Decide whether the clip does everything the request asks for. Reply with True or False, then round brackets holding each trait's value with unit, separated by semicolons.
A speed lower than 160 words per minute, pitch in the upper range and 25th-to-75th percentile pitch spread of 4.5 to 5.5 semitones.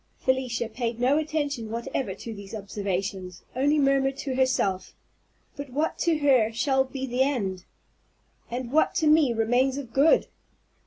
False (150 wpm; 255 Hz; 3.8 semitones)